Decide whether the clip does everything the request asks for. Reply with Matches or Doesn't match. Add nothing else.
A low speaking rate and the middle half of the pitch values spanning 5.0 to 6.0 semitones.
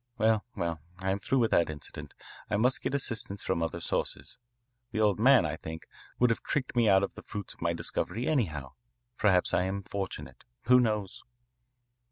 Doesn't match